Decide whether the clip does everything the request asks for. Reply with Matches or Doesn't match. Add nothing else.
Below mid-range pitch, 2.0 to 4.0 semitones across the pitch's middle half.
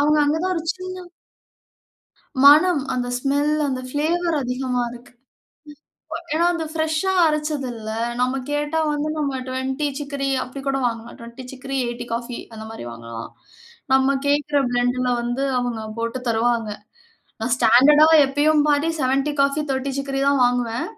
Doesn't match